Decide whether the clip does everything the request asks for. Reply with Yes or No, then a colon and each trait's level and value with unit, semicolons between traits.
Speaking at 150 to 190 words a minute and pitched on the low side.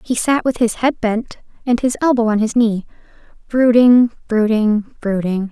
No: average, 165 wpm; high, 230 Hz